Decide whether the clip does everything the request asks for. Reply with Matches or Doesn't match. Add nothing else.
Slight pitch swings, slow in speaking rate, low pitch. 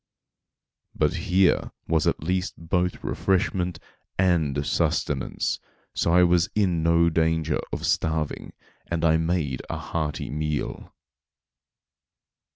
Matches